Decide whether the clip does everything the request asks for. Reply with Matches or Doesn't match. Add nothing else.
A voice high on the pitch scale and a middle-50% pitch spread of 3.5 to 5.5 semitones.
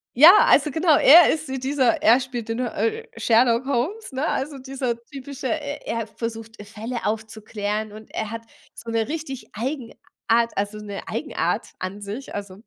Matches